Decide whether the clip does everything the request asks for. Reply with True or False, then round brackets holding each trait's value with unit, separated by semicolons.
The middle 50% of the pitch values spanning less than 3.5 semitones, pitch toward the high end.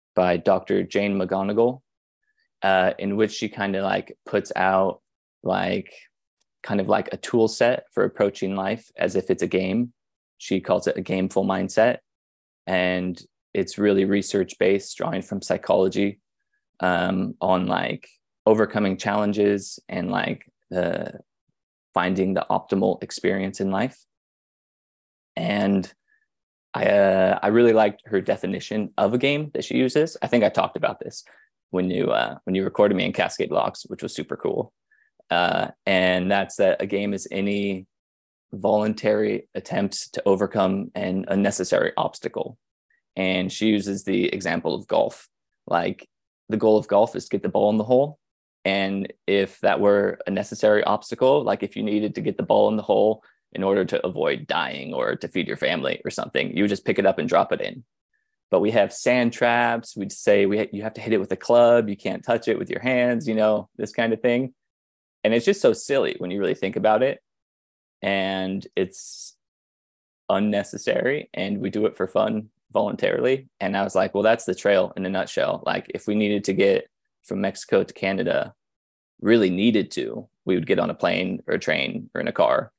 False (3.1 semitones; 100 Hz)